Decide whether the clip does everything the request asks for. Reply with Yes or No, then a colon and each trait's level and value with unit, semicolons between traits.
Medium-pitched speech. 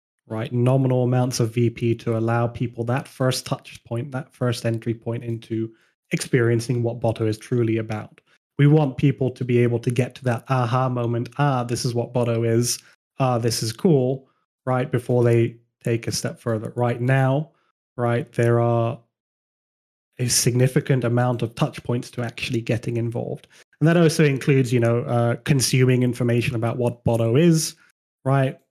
No: low, 120 Hz